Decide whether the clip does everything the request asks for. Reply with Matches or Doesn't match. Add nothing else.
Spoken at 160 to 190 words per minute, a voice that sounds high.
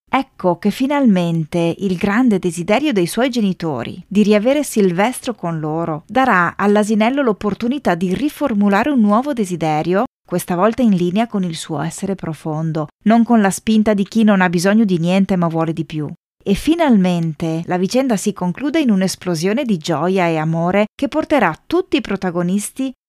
Matches